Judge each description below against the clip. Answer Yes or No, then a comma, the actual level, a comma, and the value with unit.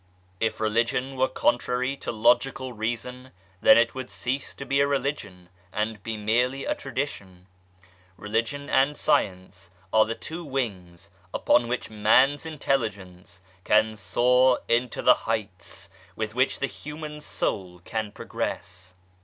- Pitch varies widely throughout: No, average, 4.3 semitones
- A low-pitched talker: Yes, low, 115 Hz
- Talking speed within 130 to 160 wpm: Yes, slow, 135 wpm